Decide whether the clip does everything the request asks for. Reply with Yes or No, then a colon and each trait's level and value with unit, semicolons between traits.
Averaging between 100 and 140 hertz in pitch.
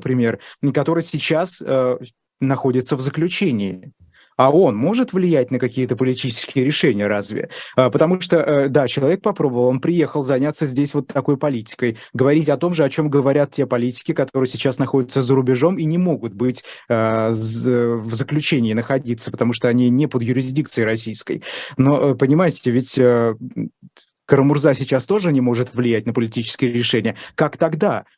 Yes: low, 135 Hz